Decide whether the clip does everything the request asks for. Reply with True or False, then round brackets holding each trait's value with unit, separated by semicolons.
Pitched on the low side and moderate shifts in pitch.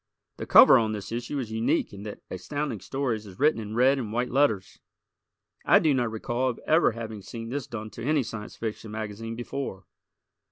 True (115 Hz; 3.4 semitones)